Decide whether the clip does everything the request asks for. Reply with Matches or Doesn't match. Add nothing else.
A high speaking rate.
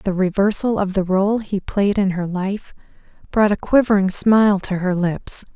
Doesn't match